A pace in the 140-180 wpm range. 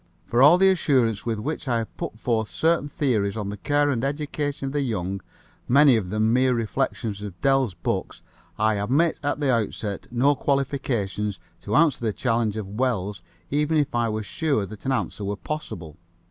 No: average, 190 wpm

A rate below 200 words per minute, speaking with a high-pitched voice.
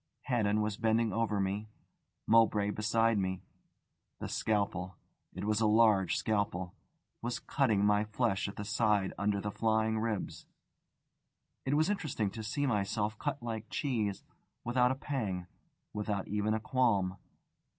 No: average, 140 wpm; low, 110 Hz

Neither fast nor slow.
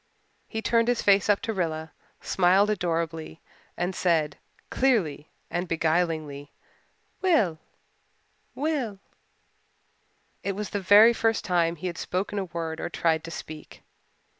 No: slow, 130 wpm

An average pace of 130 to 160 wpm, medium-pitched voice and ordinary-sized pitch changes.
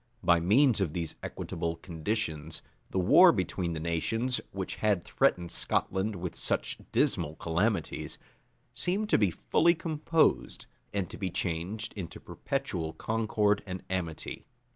No: average, 140 wpm; very low, 95 Hz; average, 4.8 semitones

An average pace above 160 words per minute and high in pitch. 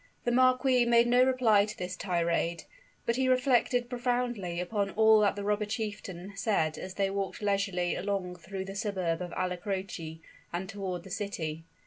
Yes: average, 170 wpm; high, 200 Hz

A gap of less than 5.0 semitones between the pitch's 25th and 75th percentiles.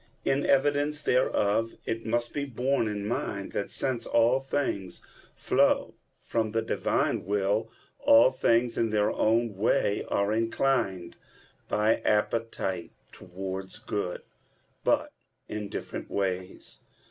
Yes: average, 3.2 semitones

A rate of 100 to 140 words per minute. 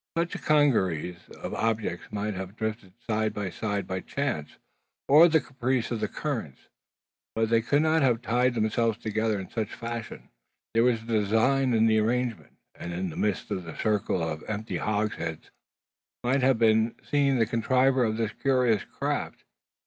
No: average, 170 wpm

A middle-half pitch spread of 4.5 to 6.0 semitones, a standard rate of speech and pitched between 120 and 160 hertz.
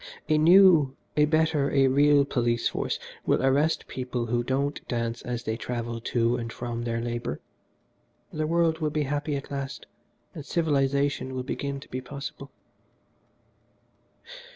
No: average, 3.7 semitones; average, 150 wpm; low, 135 Hz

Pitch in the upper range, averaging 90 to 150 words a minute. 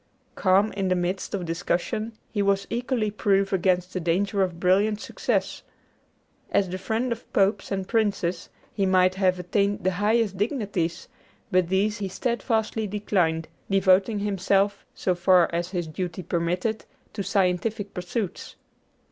Yes: high, 195 Hz; average, 145 wpm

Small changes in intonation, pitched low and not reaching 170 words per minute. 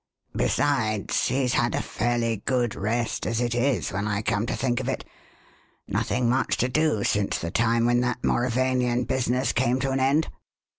No: narrow, 2.1 semitones; low, 120 Hz; average, 180 wpm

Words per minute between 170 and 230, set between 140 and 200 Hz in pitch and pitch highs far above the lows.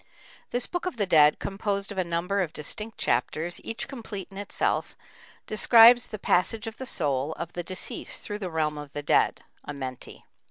Yes: average, 185 wpm; medium, 185 Hz; wide, 5.9 semitones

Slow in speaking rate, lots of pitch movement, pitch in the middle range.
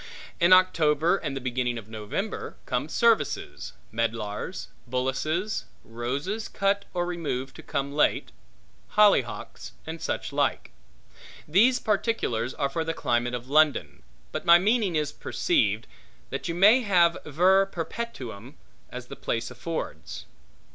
Yes: slow, 130 wpm; wide, 7.4 semitones; medium, 155 Hz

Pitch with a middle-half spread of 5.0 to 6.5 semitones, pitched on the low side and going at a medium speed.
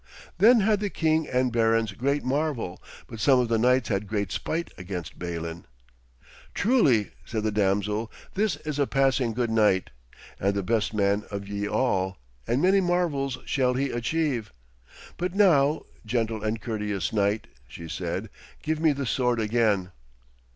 Yes: wide, 5.5 semitones; low, 115 Hz; average, 160 wpm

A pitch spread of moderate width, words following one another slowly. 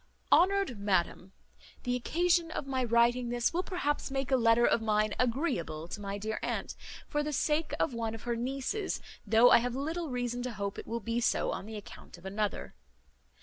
No: average, 4.2 semitones; average, 195 wpm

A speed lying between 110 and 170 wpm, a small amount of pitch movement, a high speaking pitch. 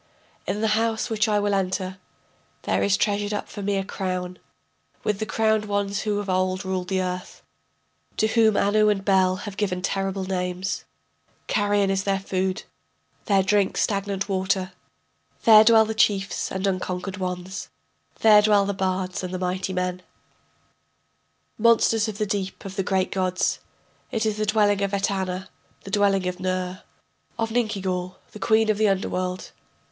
Yes: average, 165 wpm; narrow, 2.0 semitones; high, 195 Hz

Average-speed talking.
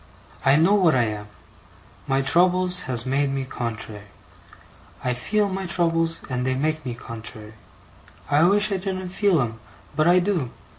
Yes: average, 160 wpm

